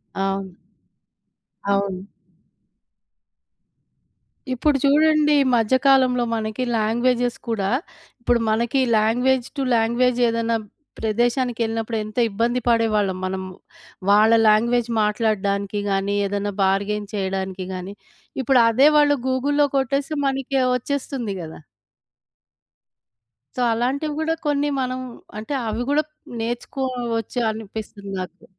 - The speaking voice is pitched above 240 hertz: No, high, 230 Hz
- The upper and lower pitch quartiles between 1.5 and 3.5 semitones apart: No, average, 3.9 semitones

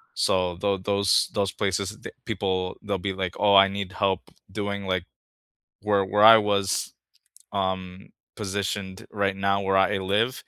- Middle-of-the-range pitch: No, low, 100 Hz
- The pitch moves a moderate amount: No, narrow, 1.3 semitones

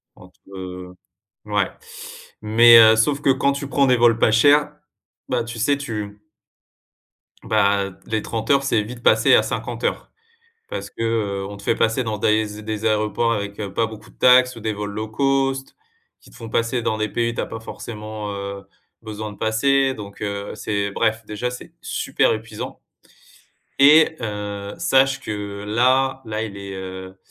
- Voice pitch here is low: Yes, low, 110 Hz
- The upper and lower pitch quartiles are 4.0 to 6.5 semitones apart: No, average, 3.4 semitones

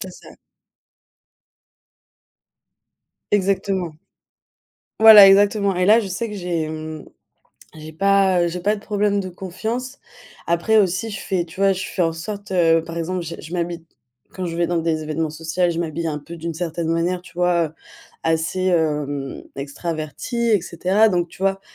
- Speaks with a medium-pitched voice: Yes, medium, 175 Hz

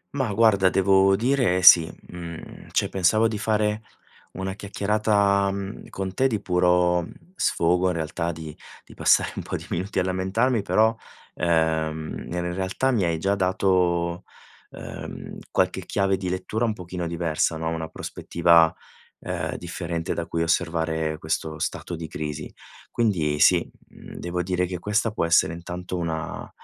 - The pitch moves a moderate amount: Yes, average, 3.0 semitones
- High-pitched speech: No, very low, 90 Hz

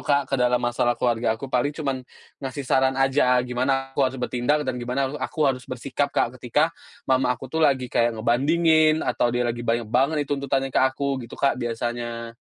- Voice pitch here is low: Yes, low, 130 Hz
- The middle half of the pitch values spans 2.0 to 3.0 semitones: Yes, narrow, 2.4 semitones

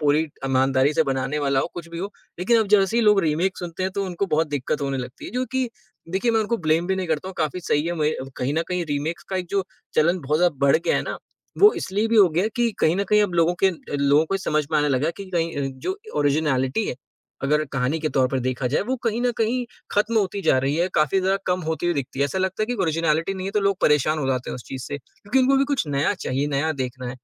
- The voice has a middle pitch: Yes, medium, 165 Hz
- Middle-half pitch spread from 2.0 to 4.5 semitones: No, average, 5.2 semitones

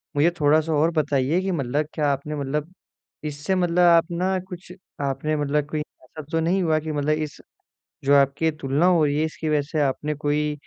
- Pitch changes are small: Yes, narrow, 2.1 semitones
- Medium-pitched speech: Yes, medium, 150 Hz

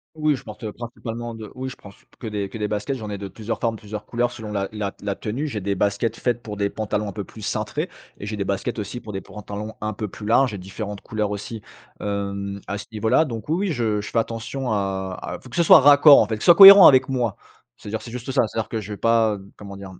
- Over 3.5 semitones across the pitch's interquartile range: No, average, 2.8 semitones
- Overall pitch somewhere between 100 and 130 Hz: Yes, low, 110 Hz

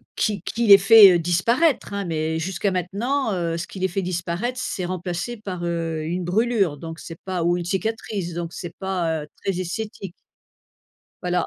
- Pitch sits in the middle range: Yes, medium, 180 Hz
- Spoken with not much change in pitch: No, average, 3.0 semitones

